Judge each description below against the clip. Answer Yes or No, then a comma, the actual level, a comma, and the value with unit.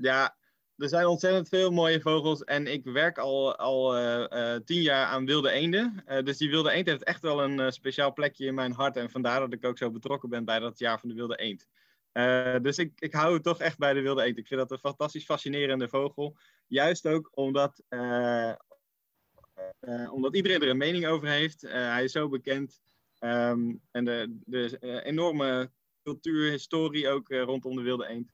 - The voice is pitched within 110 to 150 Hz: Yes, low, 135 Hz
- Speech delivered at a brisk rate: Yes, fast, 215 wpm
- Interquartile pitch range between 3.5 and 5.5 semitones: Yes, average, 3.9 semitones